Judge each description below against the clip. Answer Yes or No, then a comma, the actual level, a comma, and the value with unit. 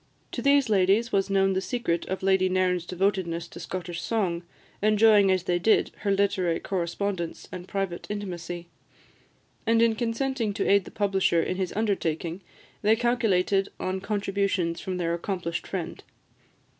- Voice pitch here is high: Yes, high, 195 Hz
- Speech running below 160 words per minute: Yes, average, 150 wpm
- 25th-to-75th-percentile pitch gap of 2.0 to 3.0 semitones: Yes, average, 2.7 semitones